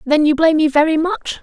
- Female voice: Yes, female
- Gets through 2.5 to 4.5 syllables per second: No, 6.3 syllables/s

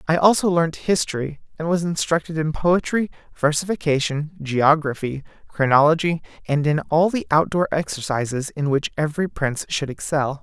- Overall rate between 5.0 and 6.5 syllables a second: Yes, 5.1 syllables/s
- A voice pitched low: No, medium, 155 Hz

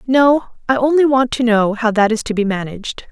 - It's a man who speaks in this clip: No, female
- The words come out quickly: Yes, fast, 230 wpm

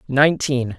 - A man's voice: Yes, male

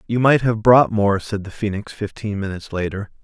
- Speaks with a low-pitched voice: Yes, low, 105 Hz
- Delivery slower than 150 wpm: No, fast, 205 wpm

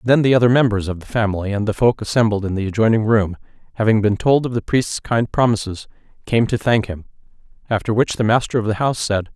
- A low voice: Yes, low, 110 Hz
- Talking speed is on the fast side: Yes, fast, 220 wpm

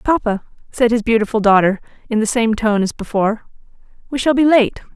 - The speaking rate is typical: Yes, average, 180 wpm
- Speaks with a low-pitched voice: No, high, 225 Hz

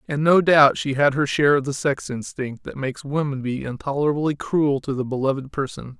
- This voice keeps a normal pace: No, fast, 210 wpm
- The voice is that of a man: Yes, male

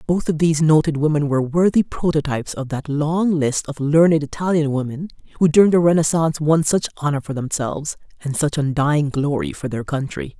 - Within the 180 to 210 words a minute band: Yes, average, 185 wpm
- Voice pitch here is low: No, medium, 150 Hz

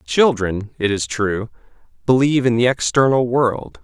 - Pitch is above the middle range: No, low, 115 Hz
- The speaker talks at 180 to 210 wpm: No, average, 140 wpm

